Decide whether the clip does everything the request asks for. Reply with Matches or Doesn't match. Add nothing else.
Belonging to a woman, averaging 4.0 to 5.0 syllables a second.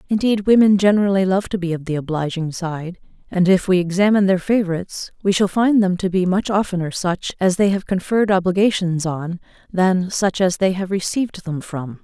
Doesn't match